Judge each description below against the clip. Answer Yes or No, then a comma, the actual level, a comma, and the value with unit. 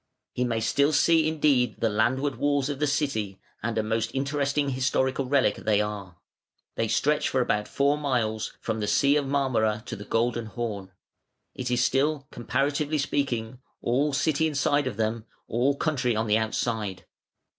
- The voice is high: No, low, 125 Hz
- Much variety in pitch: No, average, 4.2 semitones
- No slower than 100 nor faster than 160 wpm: No, average, 170 wpm